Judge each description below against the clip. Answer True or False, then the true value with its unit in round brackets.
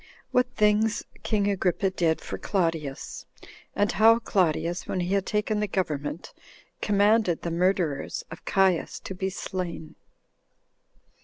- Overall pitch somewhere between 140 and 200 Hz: True (190 Hz)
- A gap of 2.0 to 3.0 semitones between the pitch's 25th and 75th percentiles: False (3.5 semitones)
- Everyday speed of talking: False (130 wpm)